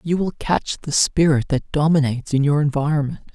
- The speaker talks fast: No, average, 180 wpm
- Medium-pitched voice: Yes, medium, 150 Hz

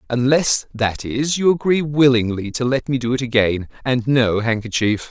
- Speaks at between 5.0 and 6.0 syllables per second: No, 4.7 syllables/s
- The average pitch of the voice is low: Yes, low, 125 Hz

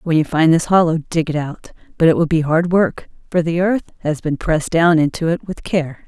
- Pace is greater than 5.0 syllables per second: Yes, 5.3 syllables/s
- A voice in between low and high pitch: Yes, medium, 165 Hz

